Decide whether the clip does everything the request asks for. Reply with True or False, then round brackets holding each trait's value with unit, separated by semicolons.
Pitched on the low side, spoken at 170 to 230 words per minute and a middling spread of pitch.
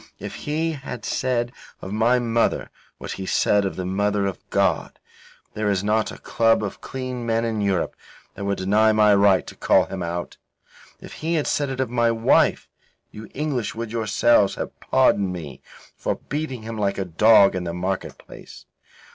True (110 Hz; 185 wpm; 3.4 semitones)